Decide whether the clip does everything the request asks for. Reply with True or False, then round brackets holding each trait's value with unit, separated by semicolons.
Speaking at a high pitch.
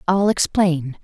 False (175 Hz)